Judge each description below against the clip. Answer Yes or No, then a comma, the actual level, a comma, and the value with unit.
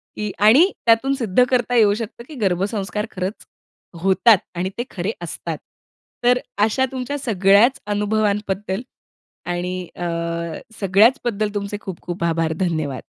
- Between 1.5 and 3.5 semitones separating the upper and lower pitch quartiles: No, average, 4.0 semitones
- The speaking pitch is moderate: No, high, 205 Hz